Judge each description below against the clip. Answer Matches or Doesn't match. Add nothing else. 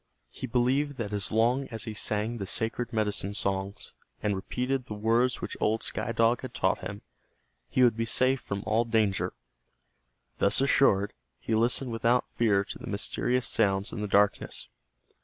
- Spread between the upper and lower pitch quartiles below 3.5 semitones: Matches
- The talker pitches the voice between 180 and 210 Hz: Doesn't match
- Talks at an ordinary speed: Matches